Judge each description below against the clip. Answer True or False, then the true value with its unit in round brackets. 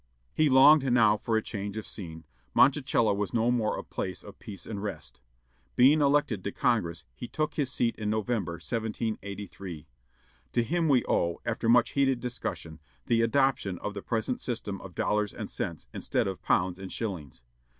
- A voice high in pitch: False (110 Hz)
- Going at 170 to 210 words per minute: True (175 wpm)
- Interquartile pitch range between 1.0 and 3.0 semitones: False (4.1 semitones)